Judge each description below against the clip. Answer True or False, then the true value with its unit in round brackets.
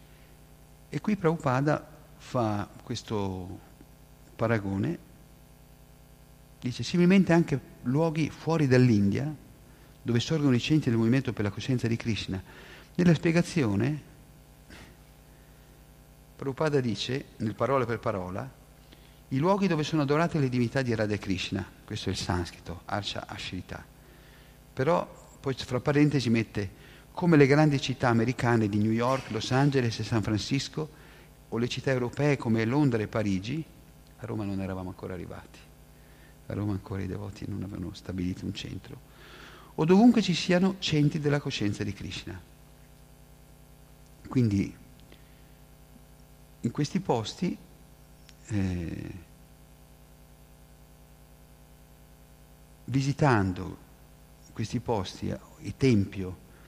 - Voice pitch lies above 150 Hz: False (135 Hz)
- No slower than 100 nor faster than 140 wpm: True (115 wpm)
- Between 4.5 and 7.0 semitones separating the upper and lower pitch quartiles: True (5.2 semitones)